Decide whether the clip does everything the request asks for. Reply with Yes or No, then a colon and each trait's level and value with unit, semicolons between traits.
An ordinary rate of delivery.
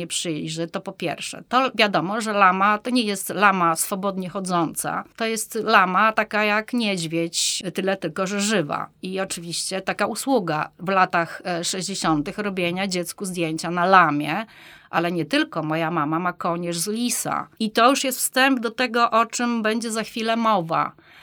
No: fast, 170 wpm